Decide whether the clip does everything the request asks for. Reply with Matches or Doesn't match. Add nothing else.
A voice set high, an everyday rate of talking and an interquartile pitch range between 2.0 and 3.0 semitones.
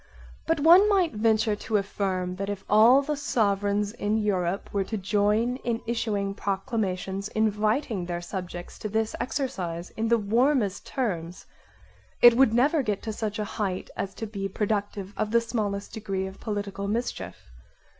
Matches